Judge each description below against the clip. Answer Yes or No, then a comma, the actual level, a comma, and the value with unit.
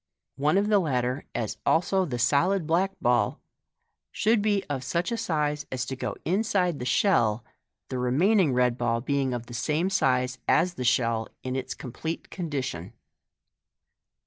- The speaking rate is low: No, average, 160 wpm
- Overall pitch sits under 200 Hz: Yes, medium, 140 Hz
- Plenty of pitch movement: Yes, wide, 6.4 semitones